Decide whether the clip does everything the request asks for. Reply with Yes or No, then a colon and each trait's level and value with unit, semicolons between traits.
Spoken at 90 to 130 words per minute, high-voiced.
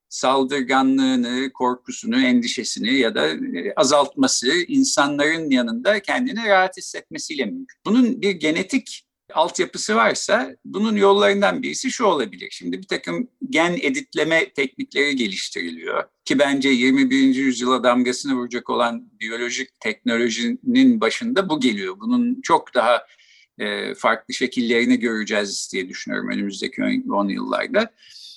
Yes: average, 110 wpm; high, 195 Hz